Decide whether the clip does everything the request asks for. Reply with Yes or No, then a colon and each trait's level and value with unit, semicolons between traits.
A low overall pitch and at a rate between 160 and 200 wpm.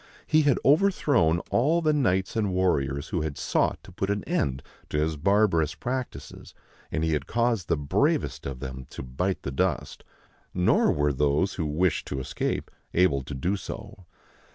Yes: very low, 85 Hz; average, 175 wpm